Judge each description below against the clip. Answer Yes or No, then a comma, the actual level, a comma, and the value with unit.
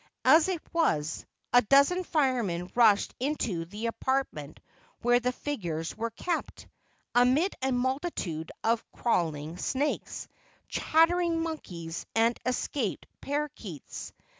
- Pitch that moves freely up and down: Yes, wide, 8.6 semitones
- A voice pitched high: Yes, high, 245 Hz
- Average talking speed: No, slow, 110 wpm